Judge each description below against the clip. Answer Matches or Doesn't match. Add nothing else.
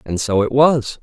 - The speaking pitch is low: Matches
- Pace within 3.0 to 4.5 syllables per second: Matches